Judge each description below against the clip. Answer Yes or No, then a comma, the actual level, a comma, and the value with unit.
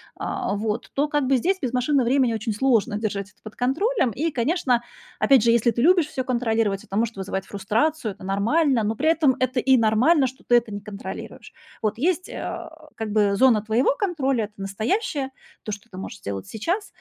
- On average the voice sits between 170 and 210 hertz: No, high, 240 Hz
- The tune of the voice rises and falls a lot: No, average, 4.7 semitones